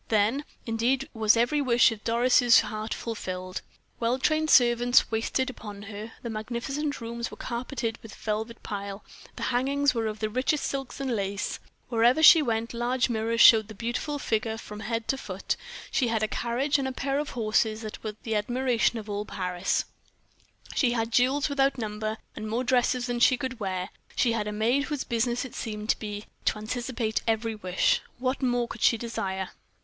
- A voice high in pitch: Yes, high, 230 Hz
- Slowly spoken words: No, average, 185 wpm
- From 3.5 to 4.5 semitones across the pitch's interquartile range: No, average, 2.9 semitones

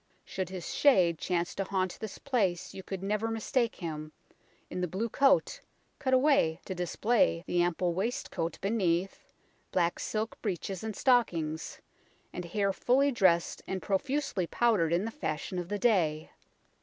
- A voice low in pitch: No, high, 190 Hz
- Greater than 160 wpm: No, average, 155 wpm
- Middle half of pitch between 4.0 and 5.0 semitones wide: Yes, average, 4.7 semitones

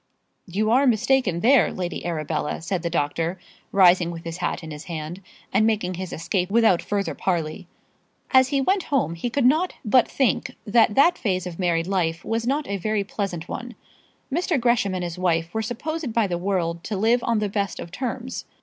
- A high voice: Yes, high, 200 Hz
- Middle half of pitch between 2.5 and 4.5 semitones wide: No, wide, 5.6 semitones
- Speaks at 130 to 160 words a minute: No, average, 195 wpm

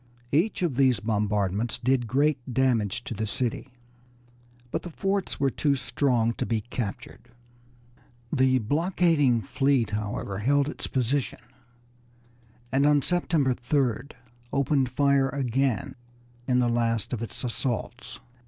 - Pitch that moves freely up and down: No, average, 3.5 semitones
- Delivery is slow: Yes, slow, 125 wpm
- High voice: No, low, 130 Hz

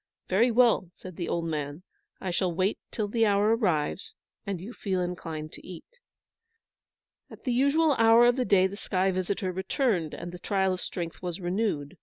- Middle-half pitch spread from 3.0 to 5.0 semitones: Yes, average, 4.4 semitones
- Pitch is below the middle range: No, high, 190 Hz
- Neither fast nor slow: Yes, average, 185 wpm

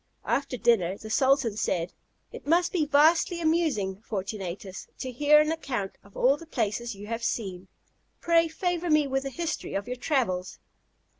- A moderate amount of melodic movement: No, wide, 7.5 semitones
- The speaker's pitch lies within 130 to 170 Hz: No, very high, 255 Hz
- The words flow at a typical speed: Yes, average, 165 wpm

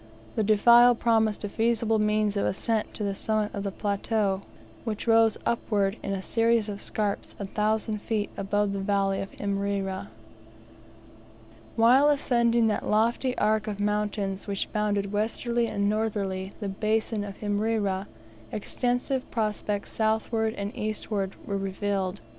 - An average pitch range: No, narrow, 1.9 semitones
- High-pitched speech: Yes, high, 210 Hz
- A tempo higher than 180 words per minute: No, average, 140 wpm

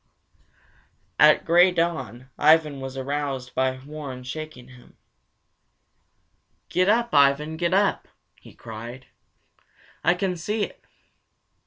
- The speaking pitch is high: No, medium, 150 Hz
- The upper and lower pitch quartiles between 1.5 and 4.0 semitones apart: No, average, 4.7 semitones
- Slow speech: Yes, slow, 110 wpm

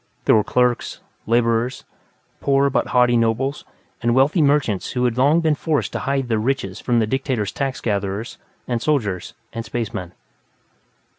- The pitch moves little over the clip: No, average, 3.4 semitones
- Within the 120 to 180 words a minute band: Yes, average, 155 wpm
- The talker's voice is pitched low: Yes, low, 120 Hz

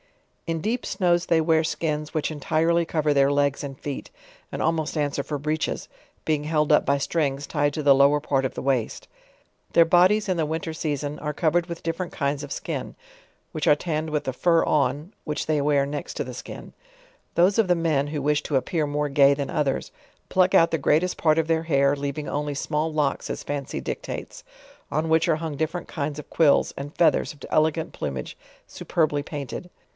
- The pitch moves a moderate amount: No, narrow, 2.3 semitones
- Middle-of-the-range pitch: Yes, medium, 150 Hz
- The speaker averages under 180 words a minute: No, fast, 205 wpm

